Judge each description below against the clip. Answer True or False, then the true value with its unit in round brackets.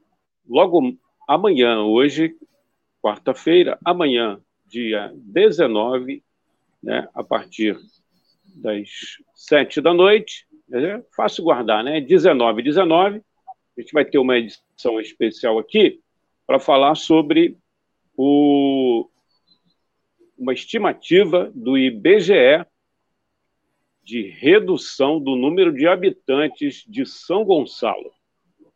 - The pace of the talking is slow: True (95 wpm)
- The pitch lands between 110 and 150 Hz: False (190 Hz)